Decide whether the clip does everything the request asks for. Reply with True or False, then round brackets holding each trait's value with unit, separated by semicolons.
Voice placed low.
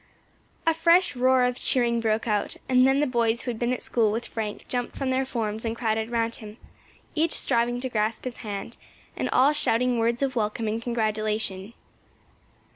False (235 Hz)